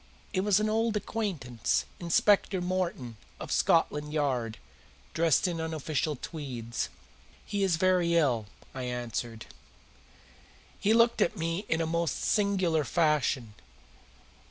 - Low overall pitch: No, medium, 165 Hz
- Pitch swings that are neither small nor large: No, wide, 6.1 semitones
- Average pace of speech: No, slow, 120 wpm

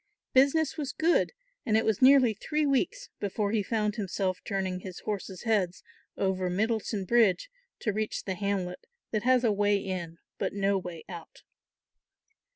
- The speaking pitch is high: Yes, high, 205 Hz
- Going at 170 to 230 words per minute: No, average, 160 wpm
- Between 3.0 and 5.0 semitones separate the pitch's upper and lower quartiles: Yes, average, 4.1 semitones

